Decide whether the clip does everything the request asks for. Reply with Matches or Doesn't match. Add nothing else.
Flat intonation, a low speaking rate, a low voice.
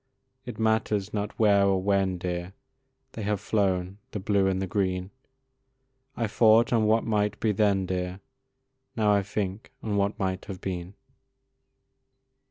Doesn't match